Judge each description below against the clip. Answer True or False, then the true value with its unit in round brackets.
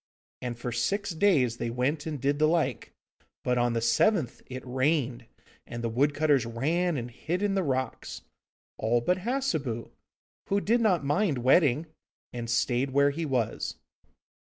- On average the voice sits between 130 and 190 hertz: True (135 Hz)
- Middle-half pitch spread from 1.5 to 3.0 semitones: False (5.6 semitones)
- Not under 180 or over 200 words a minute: False (160 wpm)